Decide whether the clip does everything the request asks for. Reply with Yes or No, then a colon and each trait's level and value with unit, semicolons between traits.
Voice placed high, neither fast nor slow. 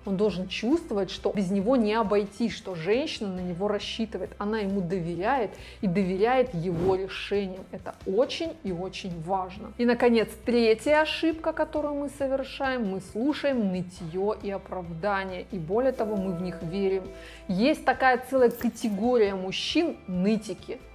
Yes: high, 210 Hz; average, 145 wpm